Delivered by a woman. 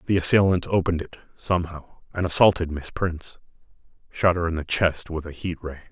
No: male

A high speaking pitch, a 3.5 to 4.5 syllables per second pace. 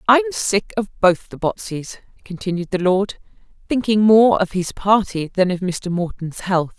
Yes: high, 195 Hz; 4.4 syllables/s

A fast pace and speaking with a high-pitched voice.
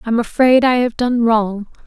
No: average, 195 wpm; high, 235 Hz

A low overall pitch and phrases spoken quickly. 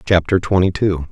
No: very low, 90 Hz; average, 160 wpm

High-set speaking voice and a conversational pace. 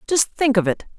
No: high, 240 Hz; fast, 245 wpm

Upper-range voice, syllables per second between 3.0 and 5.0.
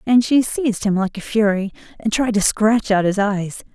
Yes: high, 215 Hz; 4.9 syllables/s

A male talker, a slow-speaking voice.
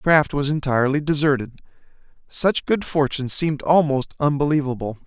Yes: male; slow, 130 wpm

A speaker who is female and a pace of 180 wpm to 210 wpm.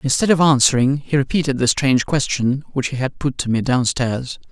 No: male; average, 200 wpm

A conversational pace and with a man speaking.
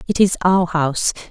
No: average, 185 wpm; female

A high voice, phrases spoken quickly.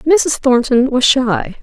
No: very high, 255 Hz; average, 150 wpm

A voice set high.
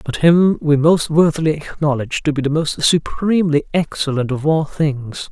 No: medium, 150 Hz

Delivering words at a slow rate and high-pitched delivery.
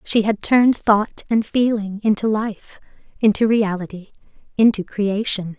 Yes: slow, 130 wpm; high, 210 Hz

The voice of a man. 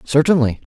Yes: male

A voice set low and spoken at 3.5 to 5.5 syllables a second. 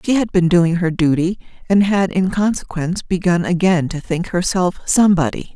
No: medium, 180 Hz; 5.1 syllables/s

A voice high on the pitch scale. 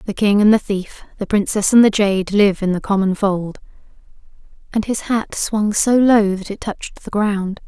Yes: high, 205 Hz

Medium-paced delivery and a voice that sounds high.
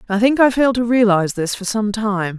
No: fast, 250 wpm; high, 215 Hz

